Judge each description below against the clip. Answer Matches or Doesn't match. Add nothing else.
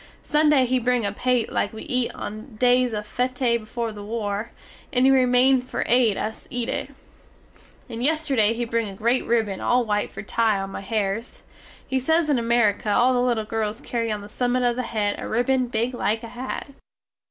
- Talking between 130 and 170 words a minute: Doesn't match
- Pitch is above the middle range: Matches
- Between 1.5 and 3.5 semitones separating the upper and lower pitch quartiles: Matches